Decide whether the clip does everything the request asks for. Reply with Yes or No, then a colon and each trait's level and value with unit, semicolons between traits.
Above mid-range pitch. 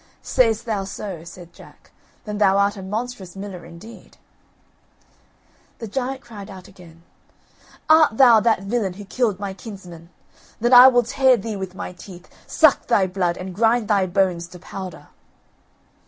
Yes: high, 200 Hz